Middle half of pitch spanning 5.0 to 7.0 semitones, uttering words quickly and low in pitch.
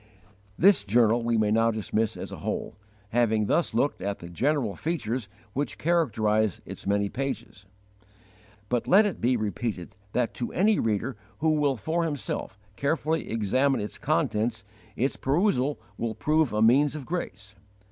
No: wide, 5.5 semitones; average, 155 wpm; low, 120 Hz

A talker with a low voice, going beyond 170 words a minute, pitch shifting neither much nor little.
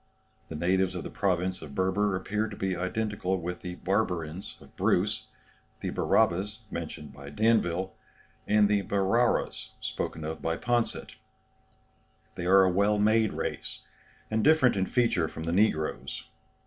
No: very low, 95 Hz; average, 150 wpm; average, 3.4 semitones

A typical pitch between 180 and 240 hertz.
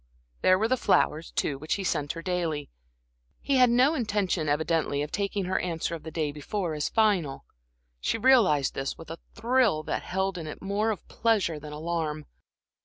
No: medium, 170 Hz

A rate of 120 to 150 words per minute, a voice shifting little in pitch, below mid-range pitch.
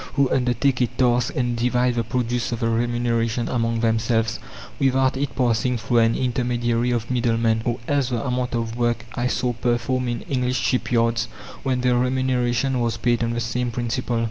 No: average, 180 wpm; narrow, 1.3 semitones; low, 120 Hz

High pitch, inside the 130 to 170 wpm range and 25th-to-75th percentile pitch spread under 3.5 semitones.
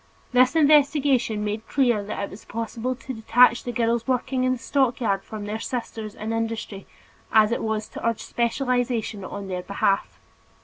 No: high, 230 Hz; average, 180 wpm; average, 2.9 semitones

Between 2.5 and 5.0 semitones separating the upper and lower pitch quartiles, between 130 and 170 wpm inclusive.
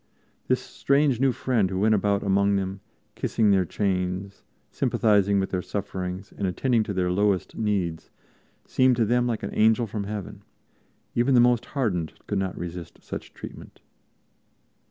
Yes: average, 3.5 semitones; average, 155 wpm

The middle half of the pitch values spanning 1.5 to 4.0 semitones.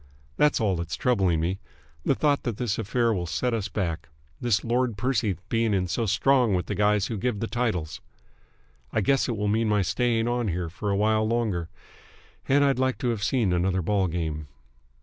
No: average, 4.4 semitones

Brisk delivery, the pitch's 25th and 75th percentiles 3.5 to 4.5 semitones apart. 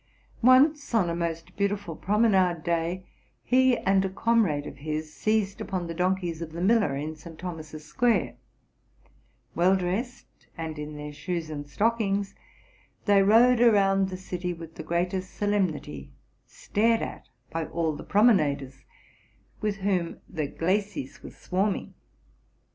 No: average, 140 wpm; average, 4.2 semitones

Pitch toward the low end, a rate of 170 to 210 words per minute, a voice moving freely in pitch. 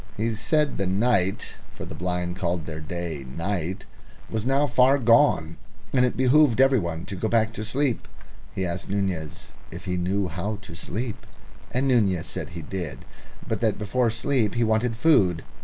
Yes: low, 100 Hz; average, 175 wpm; wide, 5.8 semitones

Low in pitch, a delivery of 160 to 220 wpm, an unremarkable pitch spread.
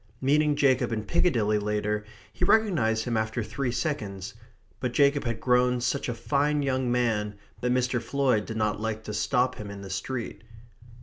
Yes: low, 120 Hz; average, 175 wpm; average, 4.0 semitones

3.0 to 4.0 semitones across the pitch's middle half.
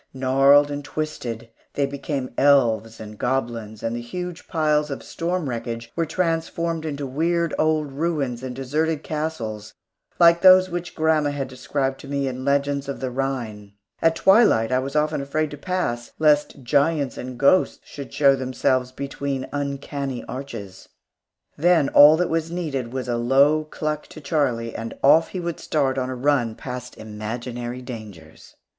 Yes: average, 3.7 semitones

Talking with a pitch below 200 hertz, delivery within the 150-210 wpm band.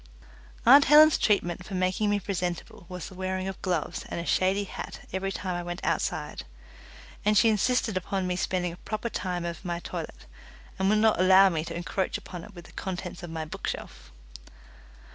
Yes: medium, 185 Hz; average, 190 wpm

